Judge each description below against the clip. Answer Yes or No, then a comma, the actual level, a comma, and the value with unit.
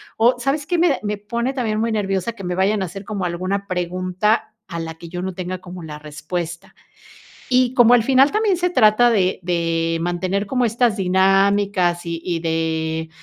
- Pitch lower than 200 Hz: Yes, high, 190 Hz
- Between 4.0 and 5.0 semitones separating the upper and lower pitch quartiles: Yes, average, 4.7 semitones